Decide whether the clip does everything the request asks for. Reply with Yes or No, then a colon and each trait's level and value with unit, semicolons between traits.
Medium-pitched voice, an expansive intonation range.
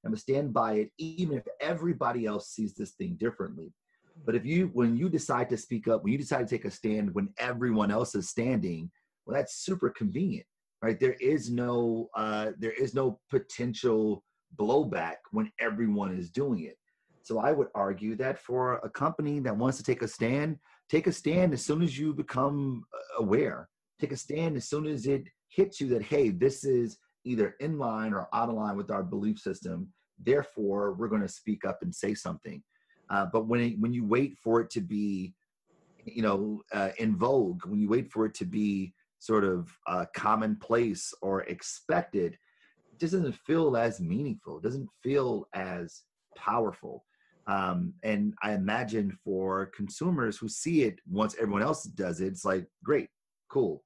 No: low, 120 Hz; wide, 6.3 semitones